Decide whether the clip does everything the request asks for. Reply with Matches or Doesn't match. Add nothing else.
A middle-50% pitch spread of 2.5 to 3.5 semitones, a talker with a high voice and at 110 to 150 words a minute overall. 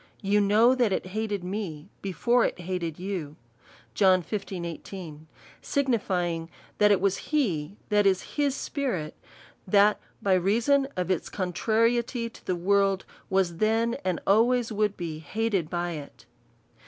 Doesn't match